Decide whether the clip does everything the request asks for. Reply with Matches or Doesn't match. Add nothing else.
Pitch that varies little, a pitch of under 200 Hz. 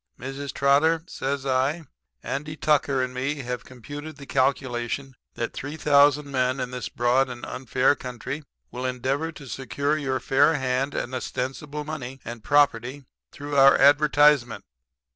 Matches